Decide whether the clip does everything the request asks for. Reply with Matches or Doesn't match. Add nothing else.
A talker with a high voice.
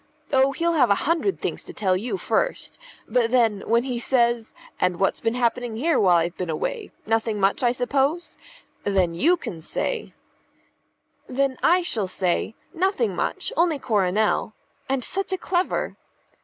Matches